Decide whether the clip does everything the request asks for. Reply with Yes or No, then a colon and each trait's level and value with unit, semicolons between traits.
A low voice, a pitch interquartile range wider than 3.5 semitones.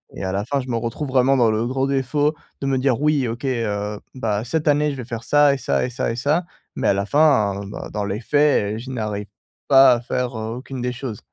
Yes: low, 125 Hz; average, 3.9 semitones